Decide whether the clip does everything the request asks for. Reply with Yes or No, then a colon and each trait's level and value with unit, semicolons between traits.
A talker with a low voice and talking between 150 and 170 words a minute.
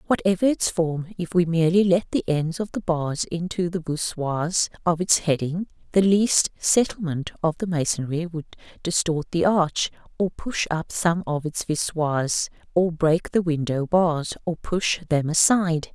No: medium, 170 Hz; average, 165 wpm